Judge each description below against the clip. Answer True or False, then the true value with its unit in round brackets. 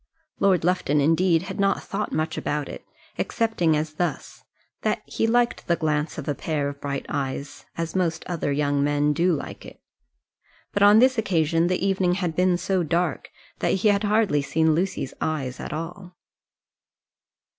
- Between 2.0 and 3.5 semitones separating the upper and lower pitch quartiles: False (4.1 semitones)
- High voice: False (165 Hz)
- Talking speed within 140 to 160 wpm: False (170 wpm)